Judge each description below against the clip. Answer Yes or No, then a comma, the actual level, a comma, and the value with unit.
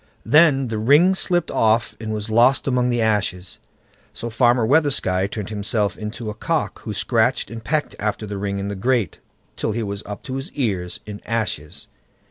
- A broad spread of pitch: No, average, 3.8 semitones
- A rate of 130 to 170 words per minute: No, average, 185 wpm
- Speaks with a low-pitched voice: Yes, low, 110 Hz